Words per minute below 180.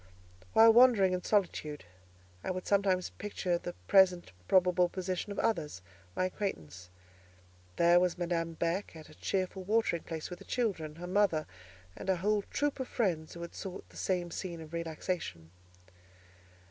Yes: average, 160 wpm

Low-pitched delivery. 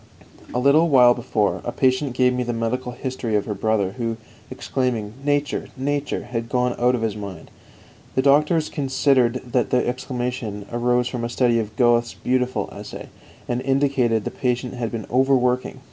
Yes: low, 125 Hz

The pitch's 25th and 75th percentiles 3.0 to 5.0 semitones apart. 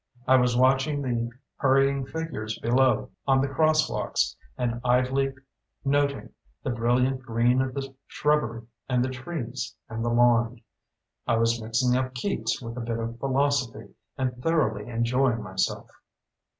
No: narrow, 2.5 semitones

